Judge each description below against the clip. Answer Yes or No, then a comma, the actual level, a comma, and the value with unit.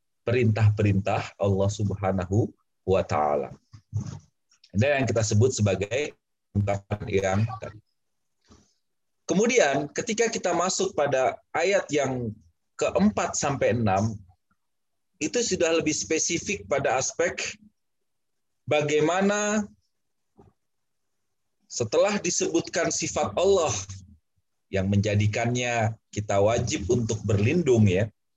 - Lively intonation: Yes, wide, 8.0 semitones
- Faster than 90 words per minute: No, slow, 85 wpm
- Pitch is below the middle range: Yes, low, 115 Hz